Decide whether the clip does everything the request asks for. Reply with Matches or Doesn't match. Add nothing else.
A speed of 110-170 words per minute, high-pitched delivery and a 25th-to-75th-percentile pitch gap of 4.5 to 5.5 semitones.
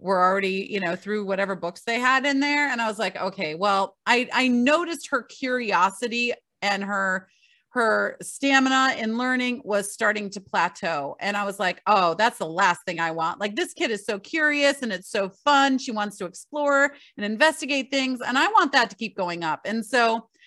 Doesn't match